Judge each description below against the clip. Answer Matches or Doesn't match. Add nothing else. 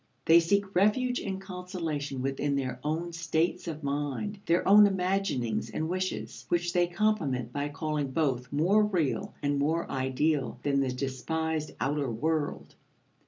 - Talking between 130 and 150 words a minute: Matches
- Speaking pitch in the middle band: Matches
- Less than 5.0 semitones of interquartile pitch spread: Matches